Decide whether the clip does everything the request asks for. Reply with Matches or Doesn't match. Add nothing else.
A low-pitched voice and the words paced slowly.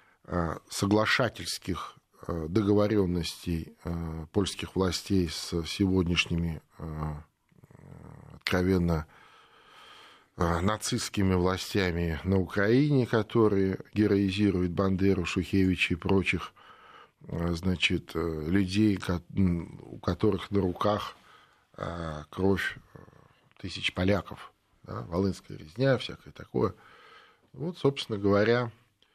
Matches